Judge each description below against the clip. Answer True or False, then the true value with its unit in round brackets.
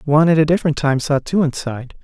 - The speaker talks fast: True (235 wpm)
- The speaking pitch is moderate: True (150 Hz)